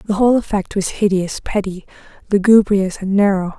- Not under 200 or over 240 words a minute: No, average, 150 wpm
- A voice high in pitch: Yes, high, 200 Hz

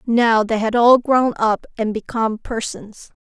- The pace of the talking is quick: No, average, 165 wpm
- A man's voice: No, female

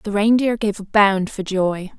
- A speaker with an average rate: No, fast, 210 wpm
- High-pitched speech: Yes, high, 205 Hz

